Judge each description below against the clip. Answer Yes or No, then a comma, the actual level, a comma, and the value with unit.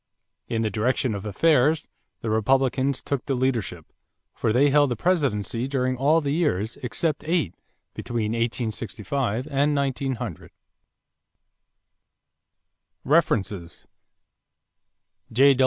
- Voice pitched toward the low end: Yes, low, 130 Hz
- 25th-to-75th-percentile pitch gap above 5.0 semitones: No, average, 4.2 semitones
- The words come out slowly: Yes, slow, 105 wpm